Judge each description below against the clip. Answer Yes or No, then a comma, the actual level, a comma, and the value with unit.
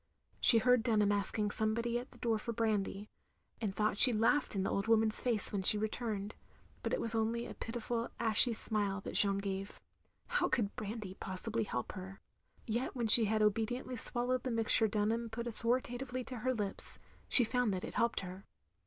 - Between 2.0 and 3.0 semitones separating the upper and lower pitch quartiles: Yes, narrow, 2.5 semitones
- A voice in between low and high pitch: No, high, 220 Hz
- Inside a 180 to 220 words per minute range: Yes, average, 190 wpm